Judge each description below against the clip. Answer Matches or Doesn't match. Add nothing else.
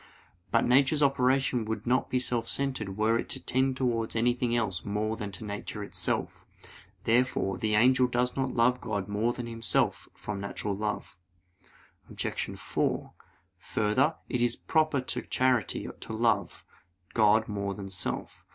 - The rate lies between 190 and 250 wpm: Doesn't match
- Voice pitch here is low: Matches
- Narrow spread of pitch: Doesn't match